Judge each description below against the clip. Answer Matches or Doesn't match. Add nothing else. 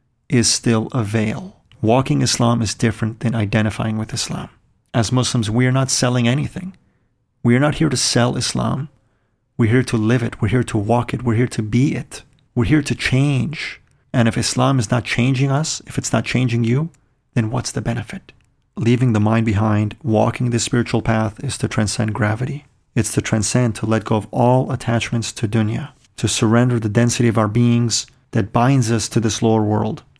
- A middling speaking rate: Matches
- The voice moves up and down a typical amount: Doesn't match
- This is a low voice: Matches